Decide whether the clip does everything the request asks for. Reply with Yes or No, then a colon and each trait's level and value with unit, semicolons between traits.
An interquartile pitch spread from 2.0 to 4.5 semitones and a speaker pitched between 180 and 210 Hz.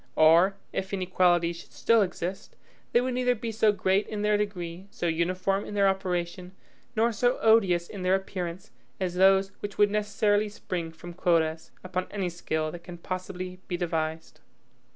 Yes: average, 2.9 semitones; medium, 185 Hz